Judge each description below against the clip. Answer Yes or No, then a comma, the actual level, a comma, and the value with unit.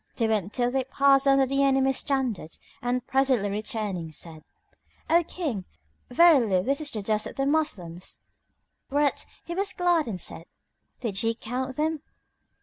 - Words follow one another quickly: No, average, 155 wpm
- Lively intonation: No, average, 4.8 semitones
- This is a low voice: No, very high, 260 Hz